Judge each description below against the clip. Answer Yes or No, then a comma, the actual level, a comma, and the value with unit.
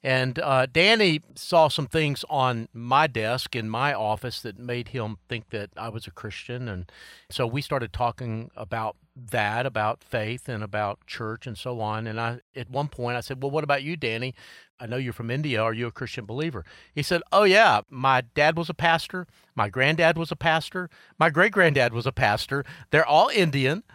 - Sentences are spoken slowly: No, fast, 205 wpm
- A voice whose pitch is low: Yes, low, 130 Hz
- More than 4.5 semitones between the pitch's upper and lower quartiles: Yes, average, 5.1 semitones